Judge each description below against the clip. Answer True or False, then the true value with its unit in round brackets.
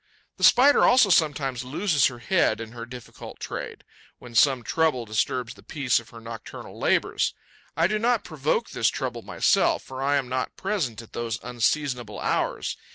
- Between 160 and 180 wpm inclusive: True (170 wpm)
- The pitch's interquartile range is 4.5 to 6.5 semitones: True (5.1 semitones)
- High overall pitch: False (130 Hz)